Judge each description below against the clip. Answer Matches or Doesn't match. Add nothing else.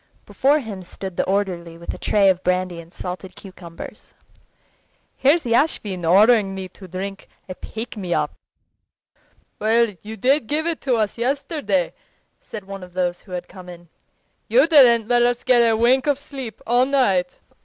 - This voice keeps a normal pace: Matches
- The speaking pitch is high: Matches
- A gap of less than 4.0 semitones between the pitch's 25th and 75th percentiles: Doesn't match